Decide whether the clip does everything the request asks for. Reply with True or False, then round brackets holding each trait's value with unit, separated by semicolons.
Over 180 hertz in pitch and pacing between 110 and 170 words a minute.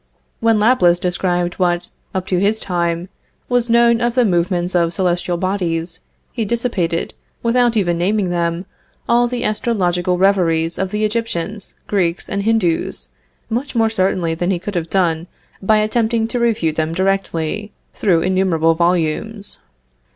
True (190 Hz; 145 wpm)